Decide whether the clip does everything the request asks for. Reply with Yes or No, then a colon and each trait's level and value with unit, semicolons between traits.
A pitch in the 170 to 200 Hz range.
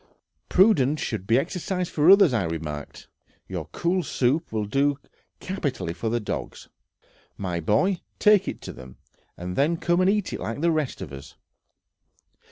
No: medium, 140 Hz